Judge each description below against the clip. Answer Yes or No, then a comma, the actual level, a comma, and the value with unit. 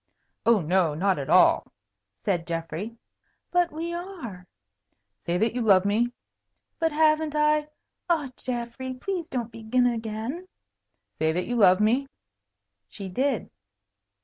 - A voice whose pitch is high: Yes, high, 235 Hz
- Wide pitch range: Yes, wide, 7.7 semitones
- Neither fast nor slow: No, slow, 130 wpm